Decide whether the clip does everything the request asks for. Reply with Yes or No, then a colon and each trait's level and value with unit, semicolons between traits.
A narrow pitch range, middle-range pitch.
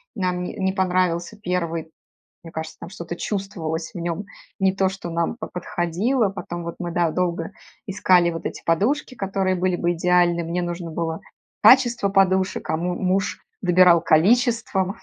Yes: narrow, 2.3 semitones; medium, 180 Hz